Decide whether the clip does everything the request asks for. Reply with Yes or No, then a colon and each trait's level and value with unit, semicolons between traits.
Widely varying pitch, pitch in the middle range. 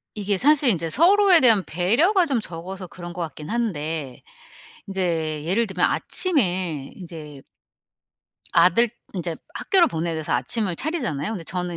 Yes: wide, 6.2 semitones; medium, 180 Hz